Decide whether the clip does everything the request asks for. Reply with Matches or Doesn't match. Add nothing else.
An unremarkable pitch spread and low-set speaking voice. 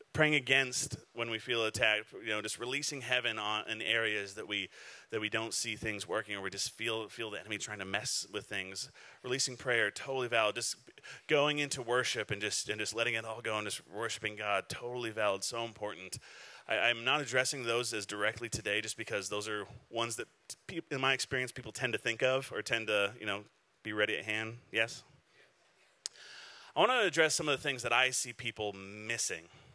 Matches